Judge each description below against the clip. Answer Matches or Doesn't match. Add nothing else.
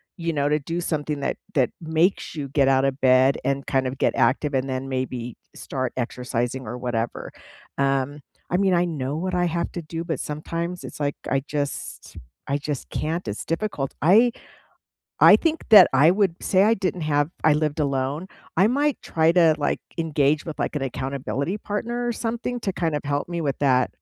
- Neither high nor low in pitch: Matches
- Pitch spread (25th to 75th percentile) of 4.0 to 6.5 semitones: Matches